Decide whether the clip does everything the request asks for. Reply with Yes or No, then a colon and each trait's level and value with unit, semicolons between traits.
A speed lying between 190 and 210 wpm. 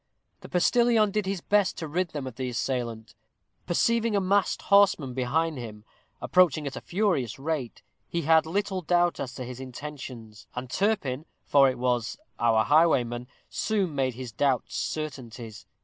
No: average, 160 wpm